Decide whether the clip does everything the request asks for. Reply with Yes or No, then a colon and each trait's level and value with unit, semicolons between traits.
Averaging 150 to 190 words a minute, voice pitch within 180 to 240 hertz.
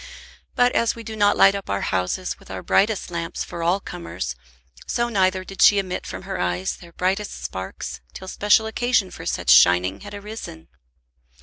Yes: average, 185 wpm; medium, 185 Hz